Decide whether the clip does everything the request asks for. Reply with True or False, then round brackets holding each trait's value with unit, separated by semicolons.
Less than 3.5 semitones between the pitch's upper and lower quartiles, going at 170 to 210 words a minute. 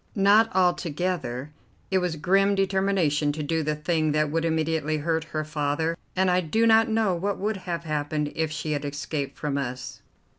False (3.8 semitones; 180 wpm)